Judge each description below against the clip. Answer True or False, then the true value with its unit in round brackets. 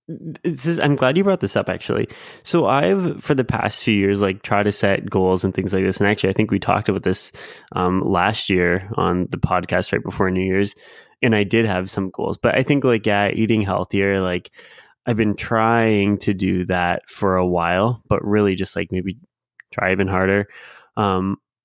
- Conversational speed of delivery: False (210 wpm)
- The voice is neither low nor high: False (100 Hz)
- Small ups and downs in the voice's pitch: False (3.3 semitones)